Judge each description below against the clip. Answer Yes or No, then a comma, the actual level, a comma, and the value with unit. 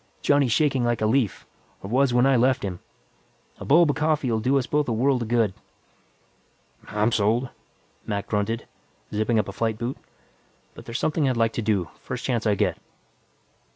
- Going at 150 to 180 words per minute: No, average, 190 wpm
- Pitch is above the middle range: No, low, 120 Hz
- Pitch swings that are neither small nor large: Yes, average, 3.6 semitones